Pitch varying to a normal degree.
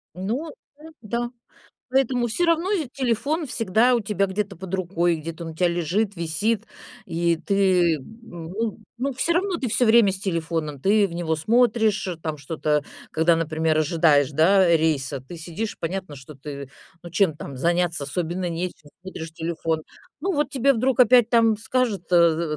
No: wide, 6.0 semitones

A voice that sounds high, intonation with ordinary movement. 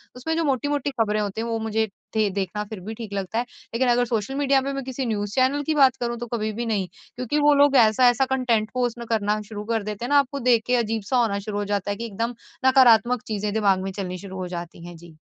Yes: high, 225 Hz; average, 3.6 semitones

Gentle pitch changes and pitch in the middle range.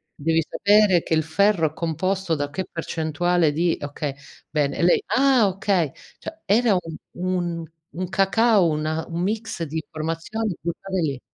No: average, 3.6 semitones; medium, 170 Hz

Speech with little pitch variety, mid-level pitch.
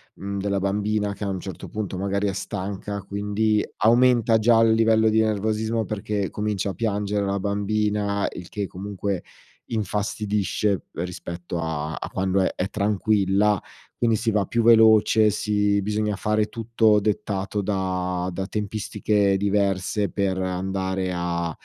No: narrow, 1.8 semitones; low, 100 Hz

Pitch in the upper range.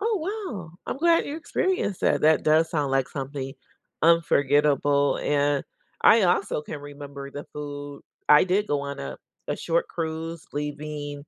No: medium, 150 Hz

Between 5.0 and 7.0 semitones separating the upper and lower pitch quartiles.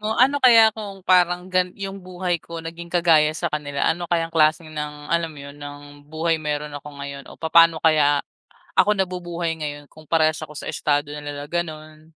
No: average, 3.0 semitones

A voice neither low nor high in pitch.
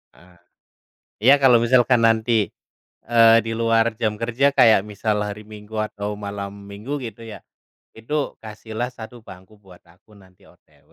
No: low, 110 Hz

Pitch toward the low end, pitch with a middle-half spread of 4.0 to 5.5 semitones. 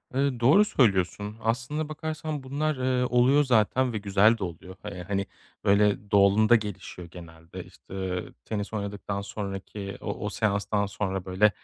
Yes: low, 105 Hz; average, 4.3 semitones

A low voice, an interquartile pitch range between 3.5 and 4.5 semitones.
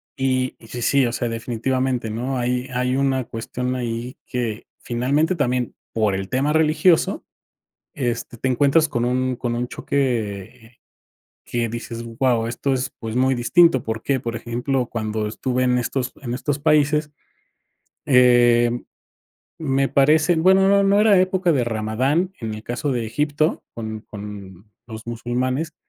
No: low, 125 Hz; average, 3.0 semitones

